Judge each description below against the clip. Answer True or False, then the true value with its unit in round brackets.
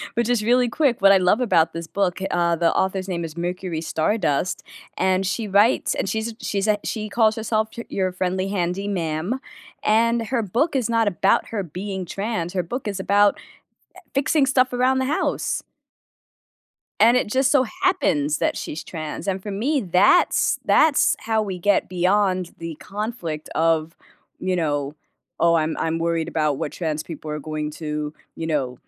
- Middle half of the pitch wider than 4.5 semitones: True (5.1 semitones)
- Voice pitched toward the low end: False (190 Hz)